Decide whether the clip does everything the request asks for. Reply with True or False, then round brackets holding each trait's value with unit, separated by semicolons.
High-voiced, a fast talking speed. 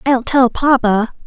False (245 Hz; 140 wpm)